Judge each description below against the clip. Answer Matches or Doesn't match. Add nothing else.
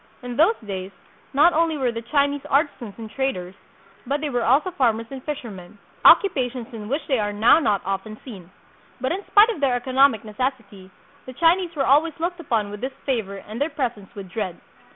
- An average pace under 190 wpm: Doesn't match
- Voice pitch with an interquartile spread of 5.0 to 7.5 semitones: Matches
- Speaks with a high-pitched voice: Matches